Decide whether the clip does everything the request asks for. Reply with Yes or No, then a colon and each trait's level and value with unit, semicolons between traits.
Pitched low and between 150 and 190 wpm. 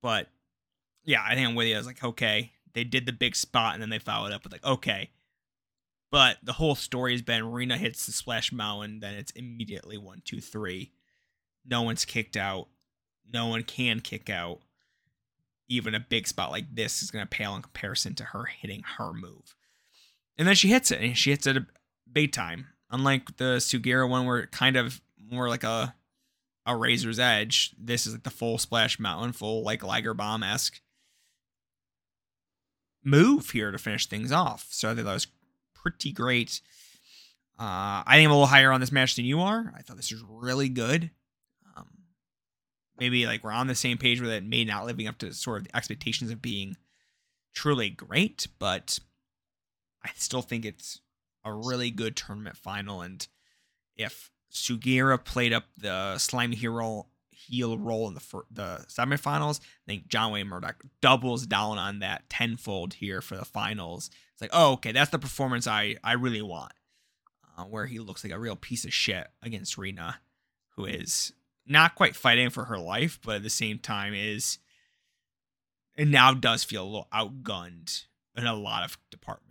Yes: low, 115 Hz; average, 185 wpm